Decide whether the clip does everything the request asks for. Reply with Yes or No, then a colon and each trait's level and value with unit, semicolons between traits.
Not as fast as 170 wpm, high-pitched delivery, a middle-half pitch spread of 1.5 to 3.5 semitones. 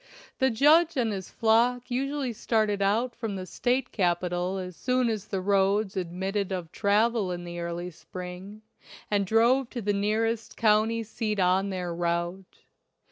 No: average, 155 wpm; high, 205 Hz; average, 3.9 semitones